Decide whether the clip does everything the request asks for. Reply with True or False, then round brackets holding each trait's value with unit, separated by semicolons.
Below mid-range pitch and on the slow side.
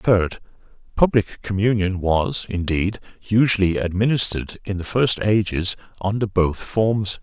True (100 Hz; 110 wpm)